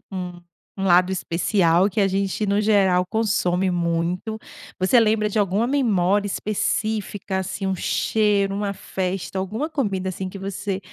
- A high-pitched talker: Yes, high, 195 Hz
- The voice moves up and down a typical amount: No, narrow, 2.3 semitones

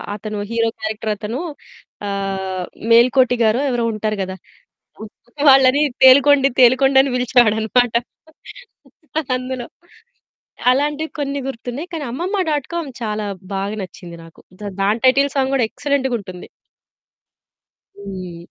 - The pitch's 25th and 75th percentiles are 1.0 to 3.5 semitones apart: No, average, 4.3 semitones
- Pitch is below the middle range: No, high, 245 Hz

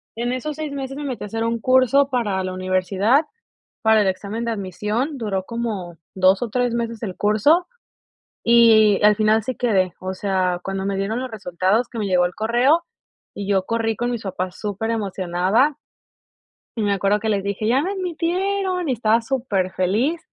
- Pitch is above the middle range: Yes, high, 220 Hz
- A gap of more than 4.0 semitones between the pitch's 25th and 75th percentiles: Yes, average, 4.5 semitones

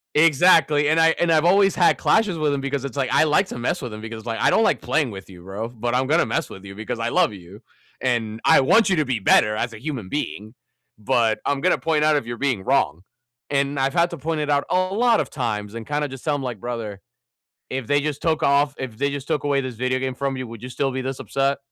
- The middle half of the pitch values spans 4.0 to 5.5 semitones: Yes, average, 4.7 semitones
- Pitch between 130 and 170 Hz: Yes, low, 135 Hz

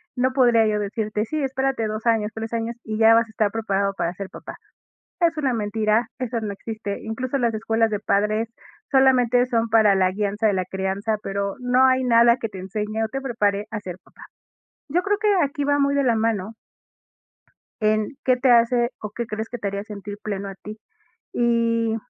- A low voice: No, high, 225 Hz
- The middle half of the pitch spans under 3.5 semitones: Yes, average, 2.8 semitones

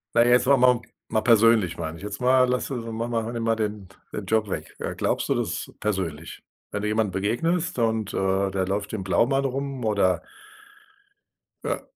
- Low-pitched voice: Yes, low, 110 Hz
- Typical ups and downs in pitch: Yes, average, 3.7 semitones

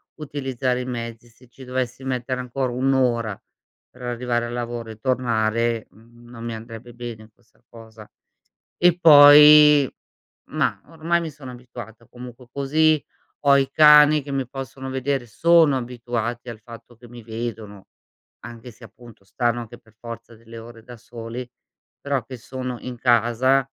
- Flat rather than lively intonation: Yes, narrow, 2.3 semitones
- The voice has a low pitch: Yes, low, 120 Hz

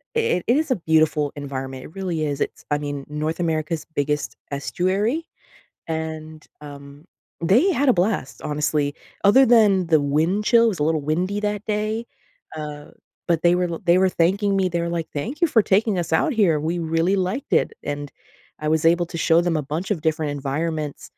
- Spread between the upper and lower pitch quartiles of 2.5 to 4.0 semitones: No, average, 4.7 semitones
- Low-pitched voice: No, medium, 165 Hz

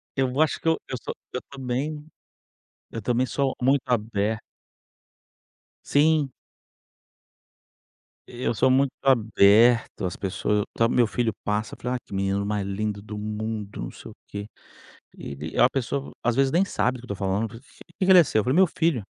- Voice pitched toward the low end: Yes, low, 120 Hz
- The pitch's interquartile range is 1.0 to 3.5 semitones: No, average, 4.2 semitones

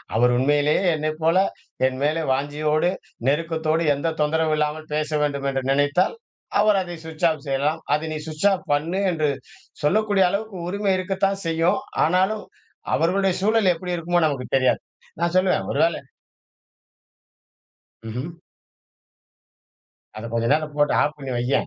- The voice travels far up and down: No, average, 3.8 semitones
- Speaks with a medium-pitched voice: Yes, medium, 155 Hz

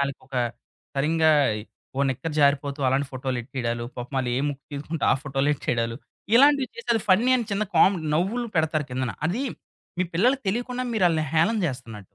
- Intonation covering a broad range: Yes, wide, 7.1 semitones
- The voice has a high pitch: No, medium, 150 Hz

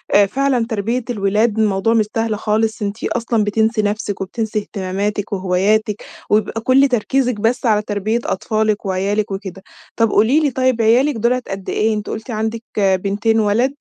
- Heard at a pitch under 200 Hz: No, high, 215 Hz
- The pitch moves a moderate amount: No, narrow, 2.1 semitones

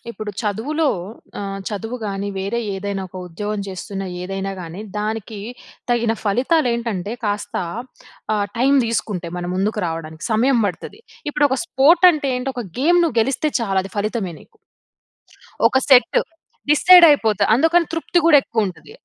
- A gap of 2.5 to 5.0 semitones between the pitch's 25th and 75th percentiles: No, wide, 5.6 semitones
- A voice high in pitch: Yes, high, 220 Hz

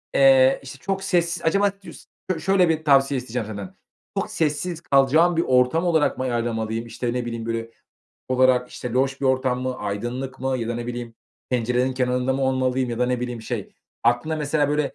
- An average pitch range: Yes, average, 3.1 semitones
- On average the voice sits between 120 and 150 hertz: Yes, low, 130 Hz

